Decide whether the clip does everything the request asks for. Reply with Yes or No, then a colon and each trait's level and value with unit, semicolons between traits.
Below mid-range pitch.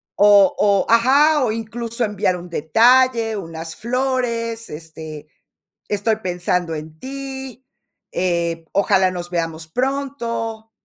No: high, 220 Hz